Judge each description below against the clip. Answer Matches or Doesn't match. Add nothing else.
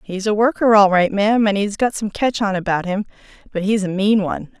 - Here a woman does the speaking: Matches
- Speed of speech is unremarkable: Doesn't match